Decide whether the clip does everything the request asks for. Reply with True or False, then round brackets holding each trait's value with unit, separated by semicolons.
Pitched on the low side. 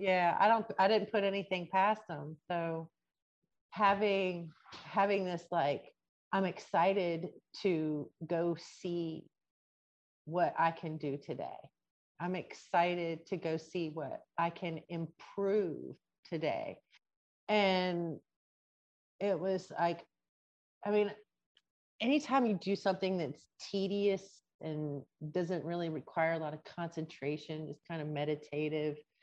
False (170 Hz)